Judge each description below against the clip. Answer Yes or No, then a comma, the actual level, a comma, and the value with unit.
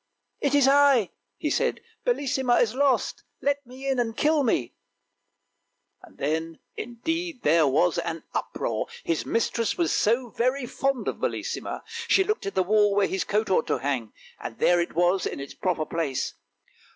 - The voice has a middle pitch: No, high, 230 Hz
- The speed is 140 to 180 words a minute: Yes, average, 175 wpm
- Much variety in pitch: Yes, wide, 8.2 semitones